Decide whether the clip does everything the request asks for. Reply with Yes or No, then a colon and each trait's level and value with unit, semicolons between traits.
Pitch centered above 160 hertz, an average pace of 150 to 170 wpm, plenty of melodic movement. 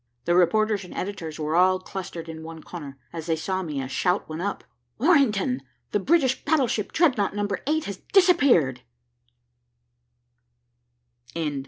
No: high, 190 Hz; average, 140 wpm; wide, 5.8 semitones